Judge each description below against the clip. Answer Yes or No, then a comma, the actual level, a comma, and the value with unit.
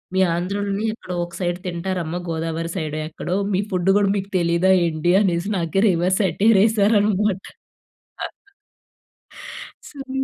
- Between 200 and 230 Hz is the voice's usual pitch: No, medium, 185 Hz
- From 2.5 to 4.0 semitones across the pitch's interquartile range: Yes, average, 2.8 semitones